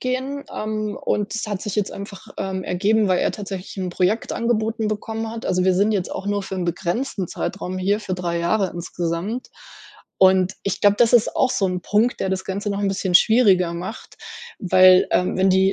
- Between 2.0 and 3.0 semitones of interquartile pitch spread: Yes, average, 2.7 semitones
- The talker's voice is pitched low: No, high, 195 Hz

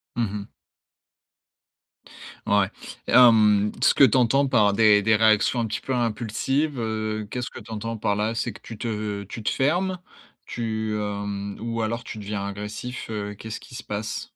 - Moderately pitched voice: No, low, 110 Hz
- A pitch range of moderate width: No, narrow, 2.2 semitones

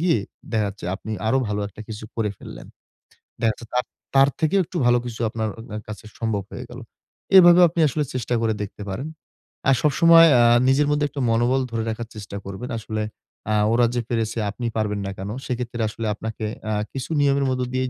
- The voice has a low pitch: Yes, low, 115 Hz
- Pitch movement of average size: Yes, average, 3.8 semitones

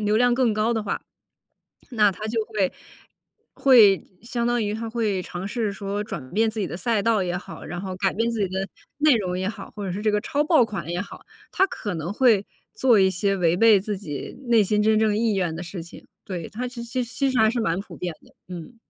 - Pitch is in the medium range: No, high, 210 Hz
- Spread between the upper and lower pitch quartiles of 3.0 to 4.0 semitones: Yes, average, 3.5 semitones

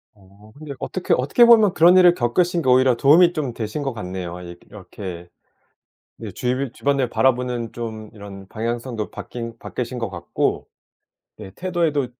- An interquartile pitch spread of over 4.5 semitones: Yes, wide, 5.4 semitones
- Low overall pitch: Yes, low, 120 Hz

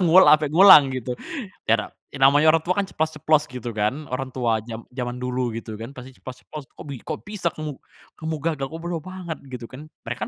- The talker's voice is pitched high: No, low, 135 Hz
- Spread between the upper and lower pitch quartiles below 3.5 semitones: No, average, 4.1 semitones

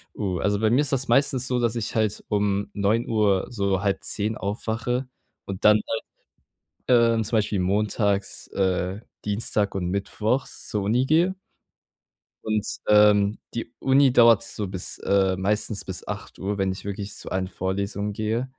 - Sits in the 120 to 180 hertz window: No, low, 105 Hz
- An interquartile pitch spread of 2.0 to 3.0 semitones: Yes, average, 2.7 semitones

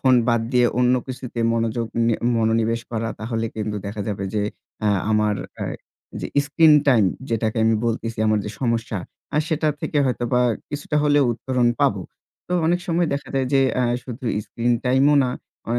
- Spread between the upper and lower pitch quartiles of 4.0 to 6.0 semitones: No, average, 3.0 semitones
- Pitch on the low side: Yes, low, 120 Hz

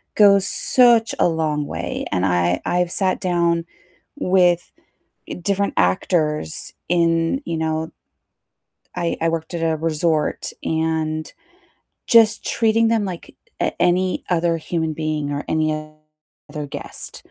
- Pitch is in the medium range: Yes, medium, 165 Hz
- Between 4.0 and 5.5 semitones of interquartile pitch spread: No, average, 2.8 semitones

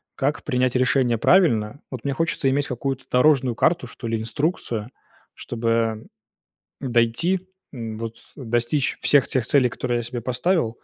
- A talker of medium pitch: No, low, 125 Hz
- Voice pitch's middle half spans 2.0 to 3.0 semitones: No, average, 3.5 semitones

